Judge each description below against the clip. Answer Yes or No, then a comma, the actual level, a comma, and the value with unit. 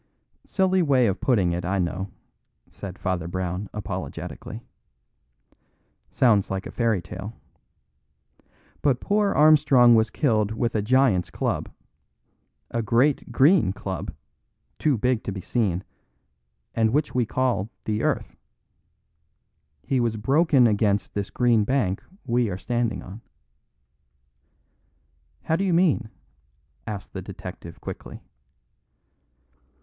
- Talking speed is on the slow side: Yes, slow, 120 wpm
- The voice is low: Yes, low, 115 Hz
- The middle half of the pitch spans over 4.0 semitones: Yes, average, 5.0 semitones